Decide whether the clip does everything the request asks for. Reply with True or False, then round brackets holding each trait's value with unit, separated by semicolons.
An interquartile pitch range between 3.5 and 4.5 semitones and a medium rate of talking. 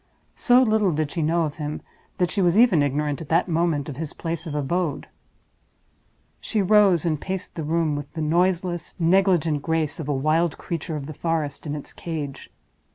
False (2.9 semitones; 190 wpm)